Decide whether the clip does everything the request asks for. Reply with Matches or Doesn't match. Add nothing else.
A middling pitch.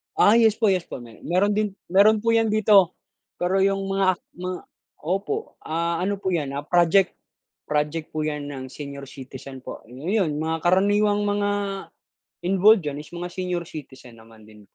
Matches